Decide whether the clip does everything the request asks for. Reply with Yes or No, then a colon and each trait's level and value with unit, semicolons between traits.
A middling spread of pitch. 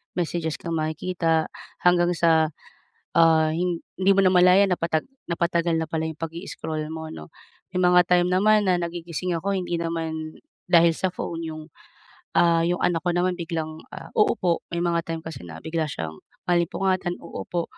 No: narrow, 1.7 semitones